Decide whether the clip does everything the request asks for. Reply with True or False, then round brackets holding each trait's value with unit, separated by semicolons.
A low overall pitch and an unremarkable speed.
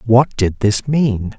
True (115 Hz; 175 wpm)